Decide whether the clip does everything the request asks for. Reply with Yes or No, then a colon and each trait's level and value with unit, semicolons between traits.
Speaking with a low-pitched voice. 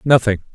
Yes: low, 110 Hz